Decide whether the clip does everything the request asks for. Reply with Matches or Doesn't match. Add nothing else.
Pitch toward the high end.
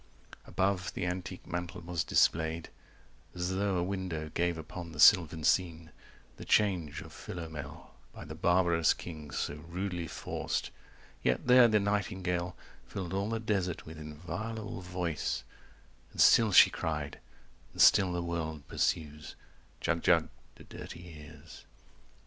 Doesn't match